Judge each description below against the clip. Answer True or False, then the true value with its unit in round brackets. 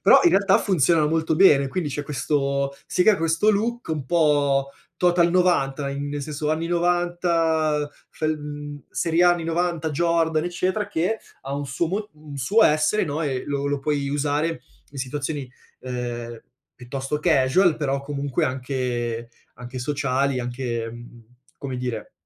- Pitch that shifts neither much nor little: True (3.7 semitones)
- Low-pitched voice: False (150 Hz)